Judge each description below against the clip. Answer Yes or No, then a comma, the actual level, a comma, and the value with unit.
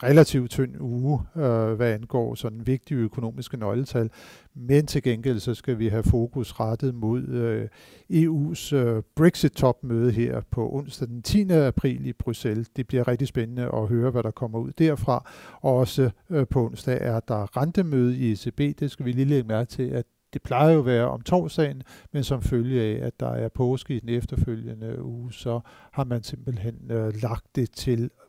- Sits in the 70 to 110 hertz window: No, low, 125 Hz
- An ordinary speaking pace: Yes, average, 185 wpm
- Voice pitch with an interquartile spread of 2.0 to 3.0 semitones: Yes, average, 2.7 semitones